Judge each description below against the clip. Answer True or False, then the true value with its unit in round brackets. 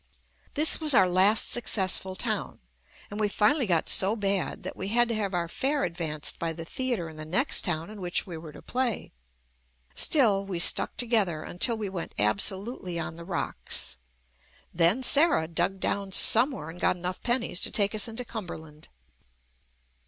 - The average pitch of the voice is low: False (195 Hz)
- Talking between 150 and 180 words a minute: True (175 wpm)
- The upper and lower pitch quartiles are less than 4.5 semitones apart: False (5.2 semitones)